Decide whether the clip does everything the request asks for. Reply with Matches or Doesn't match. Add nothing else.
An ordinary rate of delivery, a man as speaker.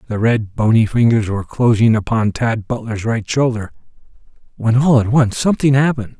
Matches